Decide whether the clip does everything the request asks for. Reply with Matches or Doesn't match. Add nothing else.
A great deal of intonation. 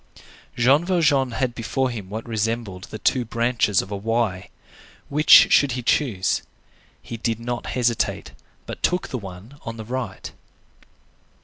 Doesn't match